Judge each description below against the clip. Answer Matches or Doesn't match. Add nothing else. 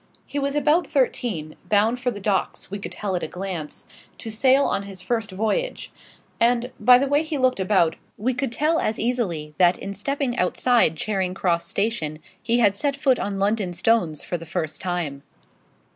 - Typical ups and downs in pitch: Doesn't match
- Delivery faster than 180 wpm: Matches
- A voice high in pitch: Matches